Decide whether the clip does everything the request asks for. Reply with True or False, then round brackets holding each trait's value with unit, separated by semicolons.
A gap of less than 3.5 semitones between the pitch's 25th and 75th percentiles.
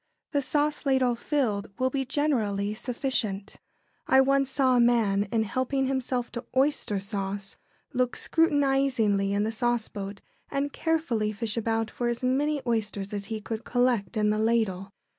False (4.2 semitones)